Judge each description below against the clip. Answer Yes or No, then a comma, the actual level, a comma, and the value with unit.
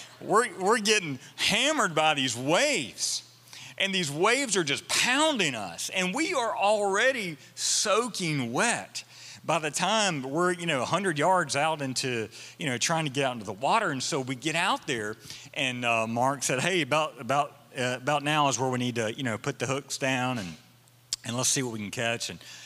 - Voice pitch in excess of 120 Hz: Yes, medium, 140 Hz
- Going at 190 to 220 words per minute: Yes, average, 200 wpm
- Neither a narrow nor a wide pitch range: No, wide, 6.1 semitones